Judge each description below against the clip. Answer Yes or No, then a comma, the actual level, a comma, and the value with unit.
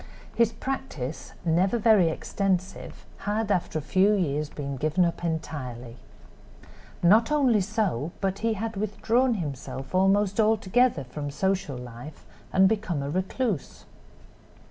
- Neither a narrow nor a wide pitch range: No, wide, 6.1 semitones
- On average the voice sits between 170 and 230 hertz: Yes, high, 190 Hz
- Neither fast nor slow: No, slow, 125 wpm